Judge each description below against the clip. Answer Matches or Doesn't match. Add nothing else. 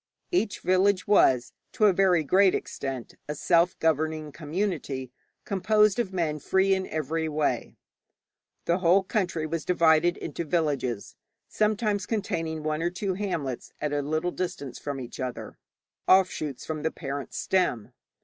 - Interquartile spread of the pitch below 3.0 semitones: Doesn't match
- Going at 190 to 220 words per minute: Doesn't match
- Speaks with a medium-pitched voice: Matches